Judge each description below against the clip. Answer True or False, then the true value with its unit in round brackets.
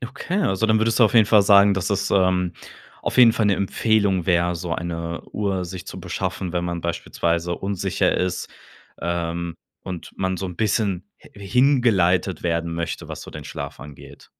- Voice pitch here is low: True (95 Hz)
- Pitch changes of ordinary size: True (3.1 semitones)